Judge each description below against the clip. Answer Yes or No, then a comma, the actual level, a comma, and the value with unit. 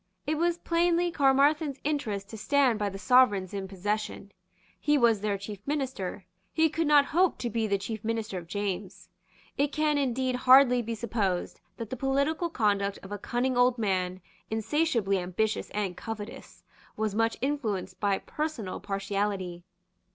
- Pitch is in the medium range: No, high, 225 Hz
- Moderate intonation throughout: No, wide, 5.8 semitones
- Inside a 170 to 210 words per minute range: No, average, 160 wpm